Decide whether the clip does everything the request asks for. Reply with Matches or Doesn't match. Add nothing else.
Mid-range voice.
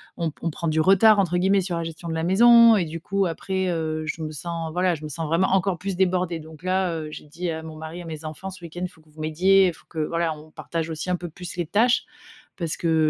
Matches